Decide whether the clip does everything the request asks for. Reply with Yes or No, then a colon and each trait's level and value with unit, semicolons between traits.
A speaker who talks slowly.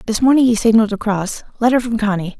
No: average, 200 wpm